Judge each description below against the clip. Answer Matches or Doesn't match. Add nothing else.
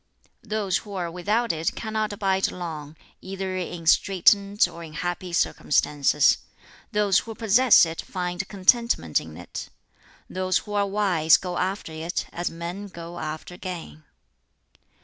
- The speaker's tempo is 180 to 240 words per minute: Doesn't match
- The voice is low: Doesn't match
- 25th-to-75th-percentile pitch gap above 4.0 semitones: Doesn't match